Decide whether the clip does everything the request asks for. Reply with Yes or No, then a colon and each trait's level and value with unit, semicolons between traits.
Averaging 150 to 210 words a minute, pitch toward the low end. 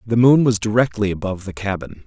Yes: fast, 205 wpm; low, 105 Hz